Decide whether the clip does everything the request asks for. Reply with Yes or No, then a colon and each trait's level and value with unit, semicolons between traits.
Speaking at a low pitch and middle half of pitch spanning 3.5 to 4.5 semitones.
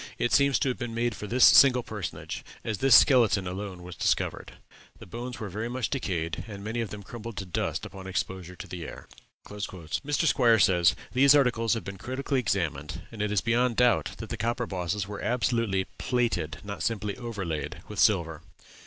Yes: low, 105 Hz; average, 4.2 semitones